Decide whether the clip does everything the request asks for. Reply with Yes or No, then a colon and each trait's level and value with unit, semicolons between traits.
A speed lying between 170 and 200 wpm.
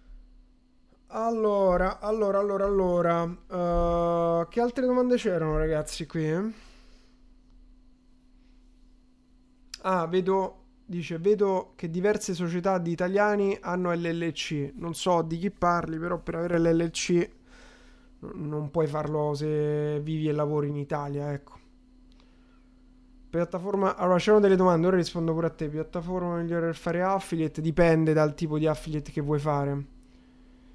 No: average, 130 wpm